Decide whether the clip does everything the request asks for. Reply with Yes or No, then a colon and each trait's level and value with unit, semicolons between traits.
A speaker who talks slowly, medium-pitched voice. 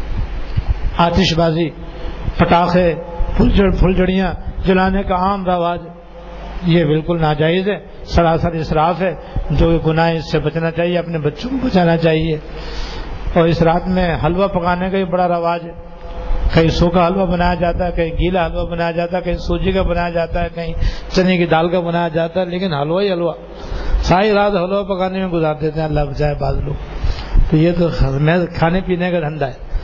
No: average, 180 wpm; medium, 170 Hz